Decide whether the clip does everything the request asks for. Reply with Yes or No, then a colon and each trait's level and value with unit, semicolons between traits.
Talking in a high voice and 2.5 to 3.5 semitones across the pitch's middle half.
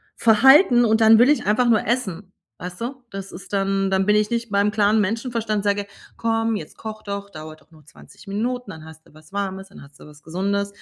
Yes: high, 205 Hz; average, 2.9 semitones